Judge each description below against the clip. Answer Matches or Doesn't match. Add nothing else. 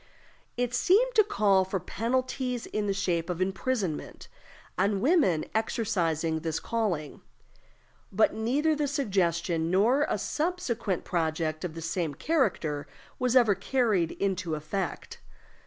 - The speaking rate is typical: Doesn't match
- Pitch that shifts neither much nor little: Doesn't match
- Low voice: Doesn't match